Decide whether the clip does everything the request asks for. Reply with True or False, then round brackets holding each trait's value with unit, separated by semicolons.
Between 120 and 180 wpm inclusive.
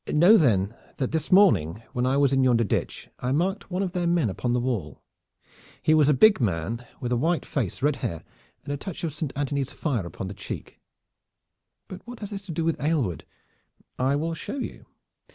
False (205 wpm)